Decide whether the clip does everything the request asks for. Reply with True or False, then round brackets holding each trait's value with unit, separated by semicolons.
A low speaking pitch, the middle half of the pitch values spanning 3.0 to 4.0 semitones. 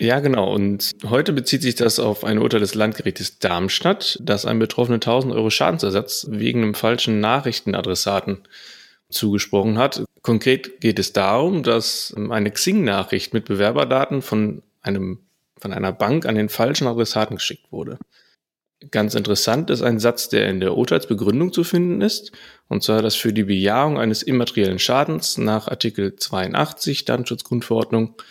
True (110 Hz; 3.3 semitones)